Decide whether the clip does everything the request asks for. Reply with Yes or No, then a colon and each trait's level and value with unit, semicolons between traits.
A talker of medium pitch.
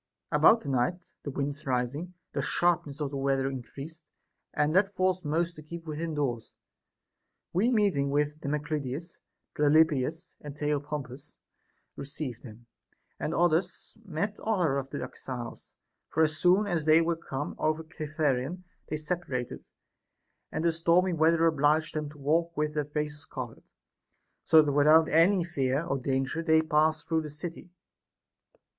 Yes: medium, 155 Hz